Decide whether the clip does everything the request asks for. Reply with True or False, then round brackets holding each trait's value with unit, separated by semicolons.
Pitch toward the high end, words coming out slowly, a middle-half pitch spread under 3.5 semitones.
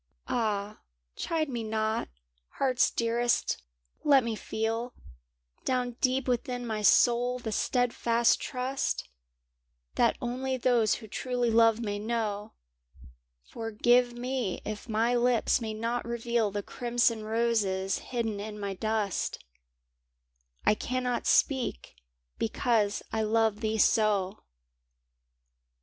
True (230 Hz; 120 wpm; 2.4 semitones)